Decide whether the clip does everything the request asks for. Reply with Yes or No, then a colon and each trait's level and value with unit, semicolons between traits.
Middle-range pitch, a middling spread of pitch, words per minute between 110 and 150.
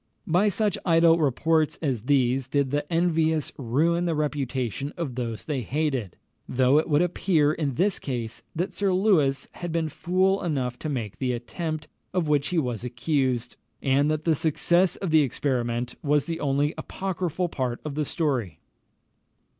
No: medium, 150 Hz; average, 4.3 semitones; average, 165 wpm